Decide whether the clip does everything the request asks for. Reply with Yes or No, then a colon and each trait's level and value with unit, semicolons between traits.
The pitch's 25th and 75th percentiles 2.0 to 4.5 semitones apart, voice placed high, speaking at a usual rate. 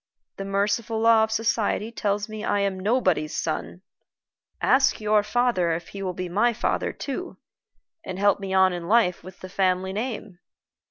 Yes: average, 3.1 semitones; high, 200 Hz; average, 170 wpm